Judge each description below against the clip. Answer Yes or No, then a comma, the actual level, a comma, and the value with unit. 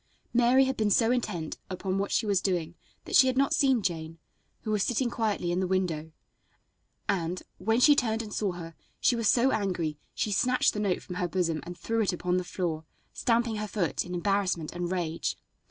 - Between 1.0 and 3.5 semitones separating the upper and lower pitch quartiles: No, average, 4.5 semitones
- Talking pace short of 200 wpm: No, fast, 205 wpm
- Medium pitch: No, high, 195 Hz